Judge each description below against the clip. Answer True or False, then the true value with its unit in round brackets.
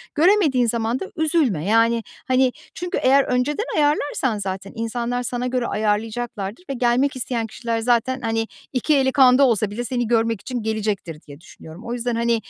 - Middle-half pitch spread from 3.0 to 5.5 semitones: False (2.6 semitones)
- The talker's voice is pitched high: True (240 Hz)